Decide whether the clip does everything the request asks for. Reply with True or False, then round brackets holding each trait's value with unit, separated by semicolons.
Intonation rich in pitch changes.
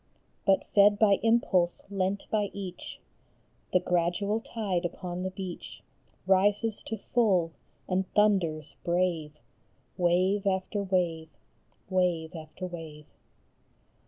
False (2.7 semitones)